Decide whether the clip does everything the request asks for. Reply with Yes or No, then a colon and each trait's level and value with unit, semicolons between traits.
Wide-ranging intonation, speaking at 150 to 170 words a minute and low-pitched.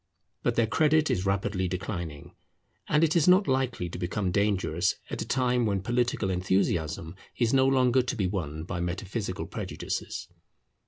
Yes: wide, 5.9 semitones; average, 160 wpm; low, 100 Hz